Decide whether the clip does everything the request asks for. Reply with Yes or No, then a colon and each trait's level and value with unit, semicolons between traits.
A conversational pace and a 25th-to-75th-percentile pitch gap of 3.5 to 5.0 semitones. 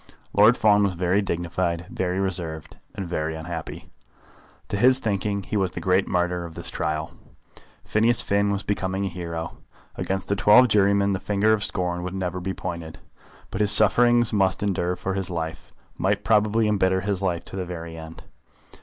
No: average, 180 wpm; average, 2.8 semitones